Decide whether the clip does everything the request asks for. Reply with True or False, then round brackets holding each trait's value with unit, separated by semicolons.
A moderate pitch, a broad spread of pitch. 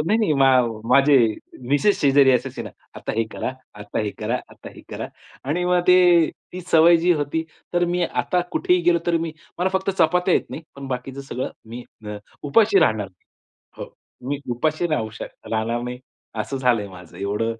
True (145 Hz; 6.6 semitones)